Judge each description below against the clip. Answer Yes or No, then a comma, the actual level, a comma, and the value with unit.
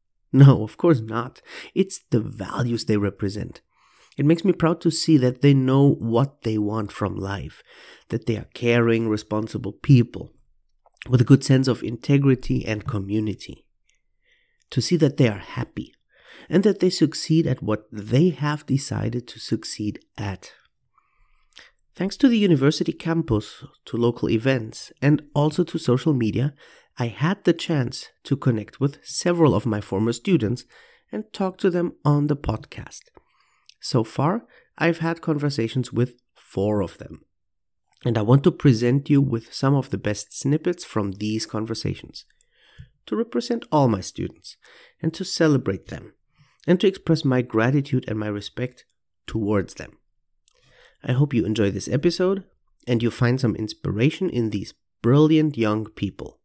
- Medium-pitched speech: No, low, 125 Hz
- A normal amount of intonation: No, wide, 6.0 semitones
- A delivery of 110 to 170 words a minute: Yes, average, 155 wpm